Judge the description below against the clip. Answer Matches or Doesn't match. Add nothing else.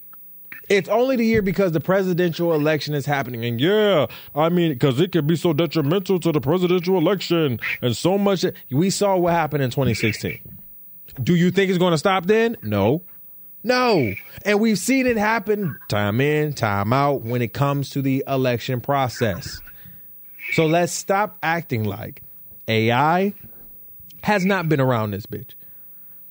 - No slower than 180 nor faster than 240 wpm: Doesn't match